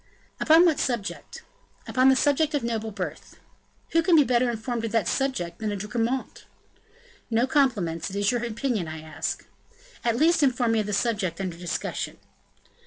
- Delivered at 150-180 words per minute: Yes, average, 175 wpm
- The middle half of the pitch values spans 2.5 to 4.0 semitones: No, average, 4.7 semitones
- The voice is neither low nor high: No, high, 230 Hz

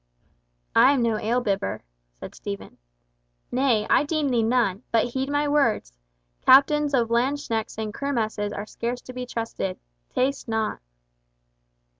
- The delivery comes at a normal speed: No, slow, 130 wpm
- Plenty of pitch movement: No, average, 4.1 semitones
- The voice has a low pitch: No, high, 235 Hz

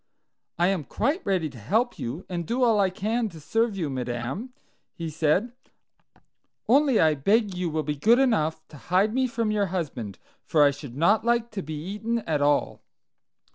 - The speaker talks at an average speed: Yes, average, 185 wpm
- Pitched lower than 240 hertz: Yes, medium, 185 Hz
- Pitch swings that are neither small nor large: No, wide, 6.9 semitones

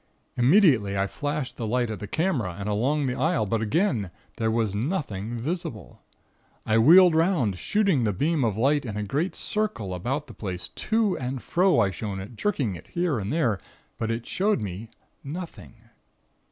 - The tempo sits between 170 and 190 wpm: Yes, average, 180 wpm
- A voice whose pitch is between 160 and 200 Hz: No, low, 120 Hz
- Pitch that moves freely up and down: Yes, wide, 7.6 semitones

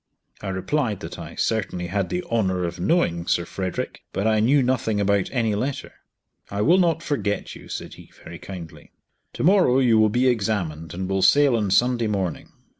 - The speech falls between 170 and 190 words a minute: Yes, average, 185 wpm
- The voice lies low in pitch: Yes, low, 105 Hz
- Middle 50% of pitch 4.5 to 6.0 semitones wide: Yes, average, 5.2 semitones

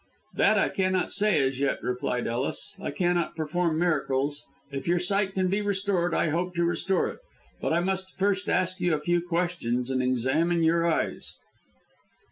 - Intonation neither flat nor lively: Yes, average, 4.2 semitones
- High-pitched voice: No, medium, 175 Hz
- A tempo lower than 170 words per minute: No, average, 175 wpm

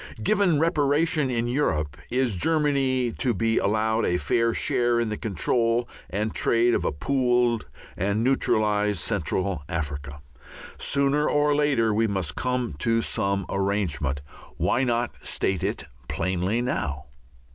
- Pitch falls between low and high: No, low, 115 Hz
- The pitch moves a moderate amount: Yes, average, 4.9 semitones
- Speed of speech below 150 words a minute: Yes, slow, 135 wpm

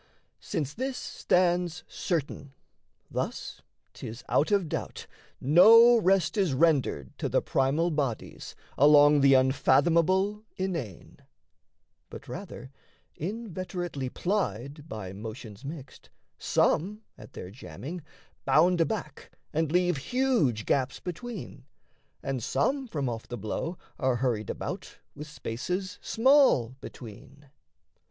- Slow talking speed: Yes, slow, 110 wpm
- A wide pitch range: Yes, wide, 5.9 semitones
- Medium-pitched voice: Yes, medium, 155 Hz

